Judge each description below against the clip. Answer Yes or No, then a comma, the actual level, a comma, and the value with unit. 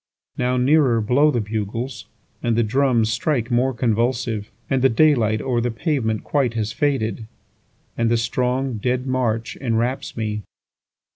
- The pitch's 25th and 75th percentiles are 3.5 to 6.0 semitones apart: No, average, 2.7 semitones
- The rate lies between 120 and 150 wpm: Yes, slow, 135 wpm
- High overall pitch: No, low, 120 Hz